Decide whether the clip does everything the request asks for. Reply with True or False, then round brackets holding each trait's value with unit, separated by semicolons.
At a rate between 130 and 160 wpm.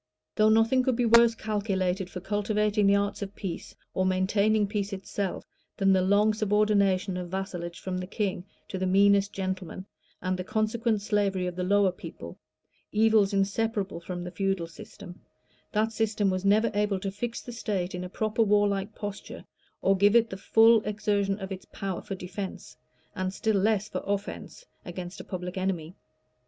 False (175 wpm)